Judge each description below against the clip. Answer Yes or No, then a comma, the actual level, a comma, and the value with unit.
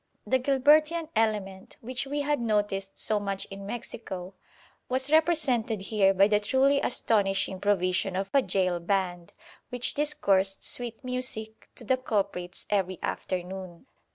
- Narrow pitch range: No, average, 4.9 semitones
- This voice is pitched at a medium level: No, high, 210 Hz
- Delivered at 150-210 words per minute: No, slow, 135 wpm